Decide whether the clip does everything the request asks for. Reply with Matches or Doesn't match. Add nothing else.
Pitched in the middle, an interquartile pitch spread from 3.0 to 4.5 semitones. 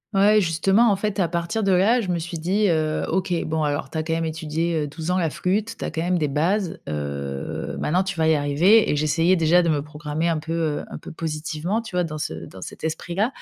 Matches